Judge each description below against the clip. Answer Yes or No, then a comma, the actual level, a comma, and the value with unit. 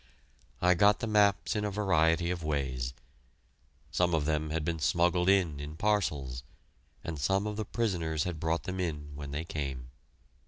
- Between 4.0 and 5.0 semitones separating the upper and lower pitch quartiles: Yes, average, 4.3 semitones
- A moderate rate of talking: Yes, average, 170 wpm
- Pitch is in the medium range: No, very low, 80 Hz